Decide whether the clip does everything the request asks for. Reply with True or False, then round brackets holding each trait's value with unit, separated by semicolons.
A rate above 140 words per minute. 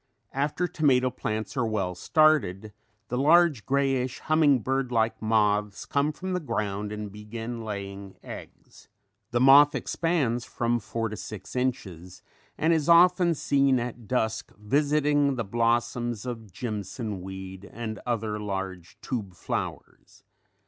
False (135 wpm)